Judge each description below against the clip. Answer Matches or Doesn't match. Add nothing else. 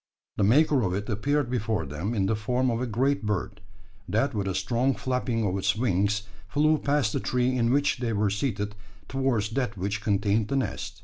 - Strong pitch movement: Doesn't match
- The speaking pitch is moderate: Doesn't match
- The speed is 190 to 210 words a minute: Matches